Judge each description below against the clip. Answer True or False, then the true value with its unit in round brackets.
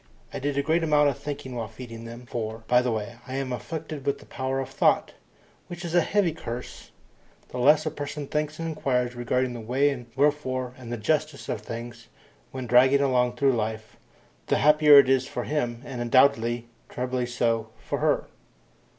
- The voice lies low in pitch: True (130 Hz)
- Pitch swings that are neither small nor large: True (3.3 semitones)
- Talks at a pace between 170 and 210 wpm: True (195 wpm)